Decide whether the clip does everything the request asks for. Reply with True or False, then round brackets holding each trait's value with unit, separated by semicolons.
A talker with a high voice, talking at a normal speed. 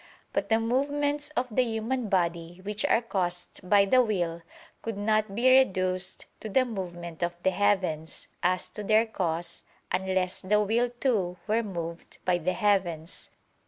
True (200 Hz; 160 wpm)